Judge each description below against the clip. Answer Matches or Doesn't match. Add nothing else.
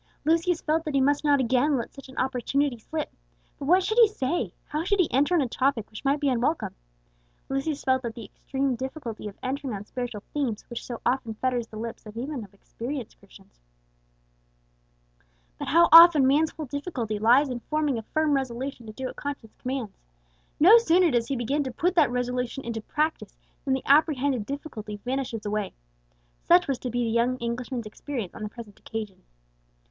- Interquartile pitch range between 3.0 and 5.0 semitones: Matches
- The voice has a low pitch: Doesn't match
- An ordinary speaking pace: Matches